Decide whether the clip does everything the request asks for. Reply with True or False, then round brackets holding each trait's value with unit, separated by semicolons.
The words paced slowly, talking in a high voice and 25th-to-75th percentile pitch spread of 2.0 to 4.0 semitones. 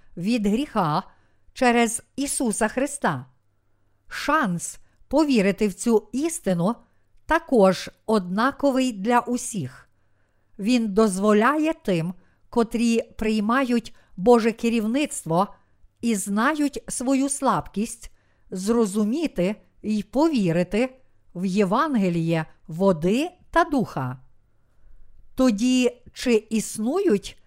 False (80 wpm; 220 Hz; 5.2 semitones)